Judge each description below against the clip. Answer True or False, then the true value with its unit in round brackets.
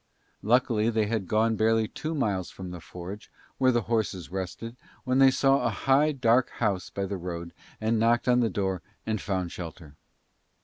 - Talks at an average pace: True (180 wpm)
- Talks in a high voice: False (110 Hz)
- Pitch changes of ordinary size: True (4.1 semitones)